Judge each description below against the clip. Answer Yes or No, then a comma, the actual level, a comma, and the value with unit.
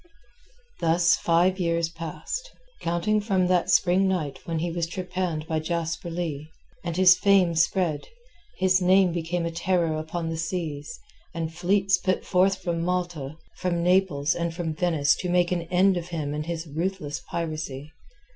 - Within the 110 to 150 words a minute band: No, average, 160 wpm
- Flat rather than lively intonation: Yes, narrow, 2.1 semitones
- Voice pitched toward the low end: No, medium, 170 Hz